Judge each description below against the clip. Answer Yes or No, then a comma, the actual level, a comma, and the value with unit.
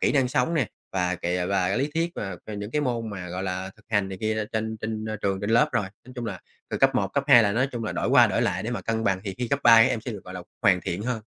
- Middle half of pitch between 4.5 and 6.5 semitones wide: No, average, 4.0 semitones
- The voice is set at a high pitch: No, low, 110 Hz